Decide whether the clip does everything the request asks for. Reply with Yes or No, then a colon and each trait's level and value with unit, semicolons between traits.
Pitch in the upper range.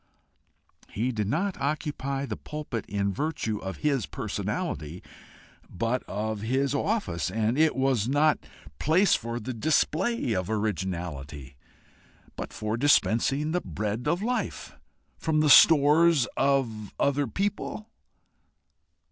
No: low, 130 Hz